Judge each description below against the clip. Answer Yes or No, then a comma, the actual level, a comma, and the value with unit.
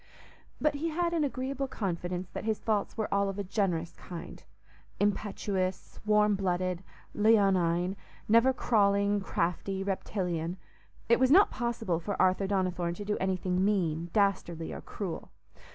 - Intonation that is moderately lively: Yes, average, 3.1 semitones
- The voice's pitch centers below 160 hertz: No, high, 195 Hz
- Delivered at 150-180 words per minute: No, slow, 135 wpm